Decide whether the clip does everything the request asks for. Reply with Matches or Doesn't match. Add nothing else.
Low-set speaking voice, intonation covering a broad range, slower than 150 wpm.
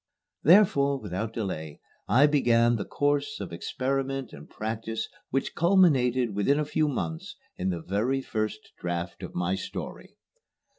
Matches